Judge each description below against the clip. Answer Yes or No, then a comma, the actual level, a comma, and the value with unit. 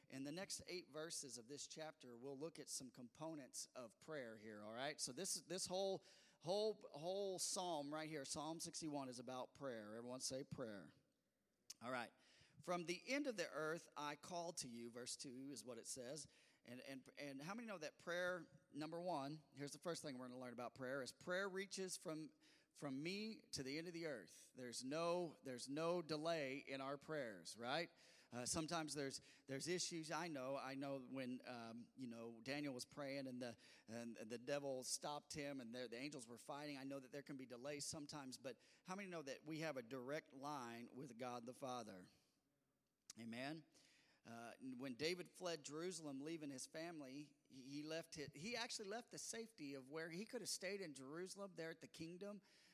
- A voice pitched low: No, medium, 145 Hz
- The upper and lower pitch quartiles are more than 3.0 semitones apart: Yes, average, 4.5 semitones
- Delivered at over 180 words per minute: Yes, average, 200 wpm